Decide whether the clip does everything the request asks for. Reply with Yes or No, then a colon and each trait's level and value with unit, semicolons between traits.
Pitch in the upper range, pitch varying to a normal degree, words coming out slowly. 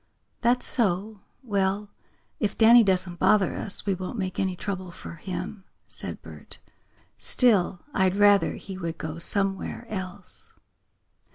No: high, 195 Hz; narrow, 2.2 semitones; slow, 130 wpm